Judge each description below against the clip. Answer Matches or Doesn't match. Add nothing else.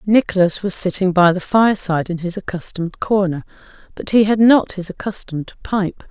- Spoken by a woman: Matches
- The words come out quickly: Doesn't match